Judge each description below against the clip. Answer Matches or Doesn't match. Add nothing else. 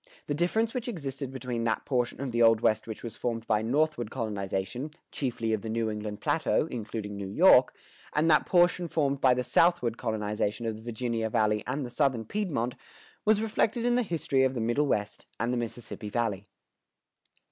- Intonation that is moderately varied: Matches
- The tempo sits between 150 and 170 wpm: Doesn't match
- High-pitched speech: Doesn't match